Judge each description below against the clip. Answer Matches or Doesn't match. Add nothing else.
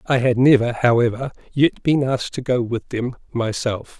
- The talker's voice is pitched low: Matches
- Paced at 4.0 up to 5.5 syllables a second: Matches